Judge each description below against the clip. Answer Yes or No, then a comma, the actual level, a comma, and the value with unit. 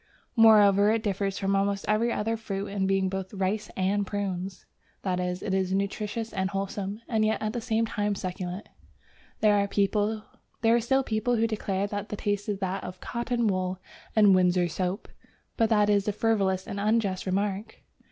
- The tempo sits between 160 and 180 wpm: Yes, average, 175 wpm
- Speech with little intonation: Yes, narrow, 2.1 semitones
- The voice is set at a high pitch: Yes, high, 200 Hz